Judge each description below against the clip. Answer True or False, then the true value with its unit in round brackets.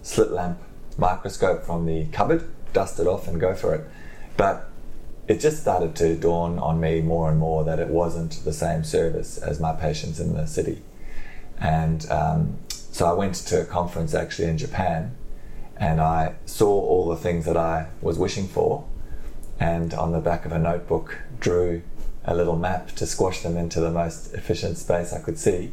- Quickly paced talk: False (185 wpm)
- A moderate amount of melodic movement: False (1.3 semitones)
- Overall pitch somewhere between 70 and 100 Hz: True (85 Hz)